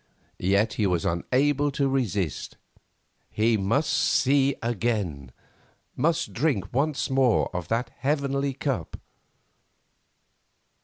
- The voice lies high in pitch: No, low, 125 Hz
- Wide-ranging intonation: Yes, wide, 5.9 semitones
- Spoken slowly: Yes, slow, 100 wpm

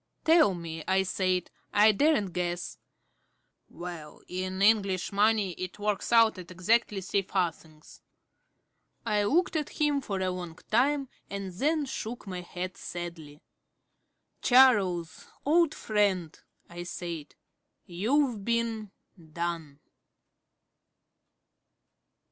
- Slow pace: Yes, slow, 110 wpm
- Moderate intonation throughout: Yes, average, 4.4 semitones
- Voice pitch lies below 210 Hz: Yes, high, 190 Hz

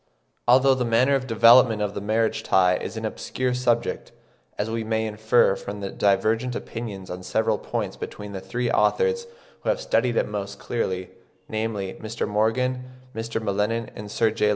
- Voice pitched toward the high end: No, low, 110 Hz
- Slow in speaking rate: No, average, 175 wpm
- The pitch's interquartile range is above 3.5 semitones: No, average, 2.7 semitones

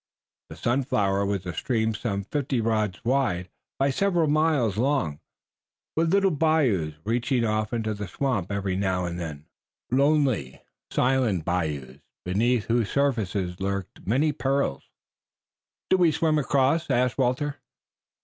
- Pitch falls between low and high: No, low, 115 Hz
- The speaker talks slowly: Yes, slow, 130 wpm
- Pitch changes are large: Yes, wide, 6.2 semitones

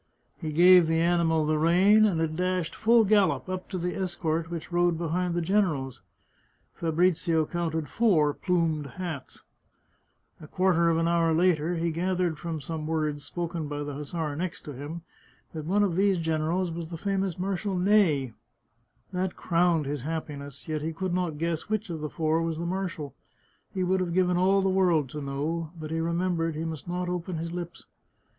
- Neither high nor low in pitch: Yes, medium, 170 Hz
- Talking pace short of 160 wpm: No, average, 185 wpm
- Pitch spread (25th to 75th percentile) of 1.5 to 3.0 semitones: Yes, narrow, 2.5 semitones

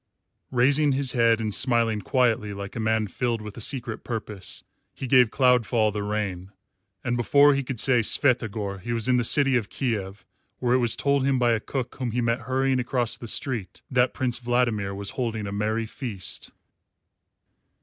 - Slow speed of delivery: No, average, 185 wpm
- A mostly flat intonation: No, average, 3.0 semitones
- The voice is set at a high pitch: No, low, 120 Hz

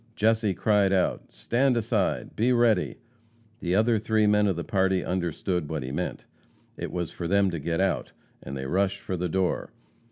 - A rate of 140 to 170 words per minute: No, average, 185 wpm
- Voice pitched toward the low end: Yes, very low, 95 Hz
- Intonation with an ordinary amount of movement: Yes, average, 3.7 semitones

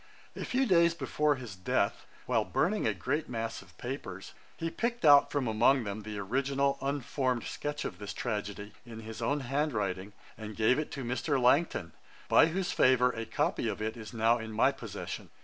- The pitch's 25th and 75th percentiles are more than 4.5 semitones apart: Yes, average, 4.9 semitones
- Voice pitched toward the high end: No, low, 125 Hz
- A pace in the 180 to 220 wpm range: Yes, average, 190 wpm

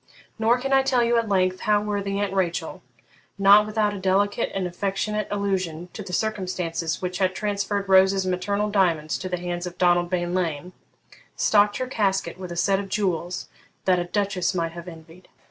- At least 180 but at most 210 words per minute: Yes, average, 185 wpm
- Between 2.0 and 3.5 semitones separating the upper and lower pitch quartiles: Yes, narrow, 2.5 semitones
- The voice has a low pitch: No, high, 190 Hz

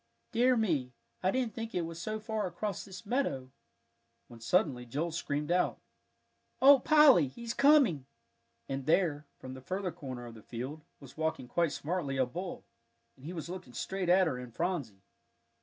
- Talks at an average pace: Yes, average, 175 wpm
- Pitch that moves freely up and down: Yes, wide, 6.7 semitones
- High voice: No, medium, 170 Hz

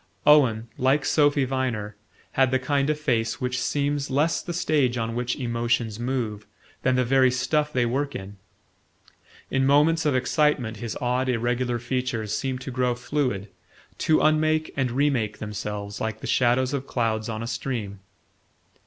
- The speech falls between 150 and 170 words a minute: Yes, average, 160 wpm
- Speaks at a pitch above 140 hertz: No, low, 125 Hz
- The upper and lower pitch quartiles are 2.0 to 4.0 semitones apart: Yes, average, 3.4 semitones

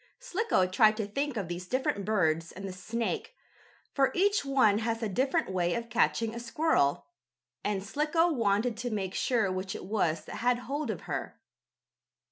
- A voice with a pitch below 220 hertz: No, high, 225 Hz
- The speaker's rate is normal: Yes, average, 175 wpm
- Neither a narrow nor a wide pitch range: No, wide, 5.9 semitones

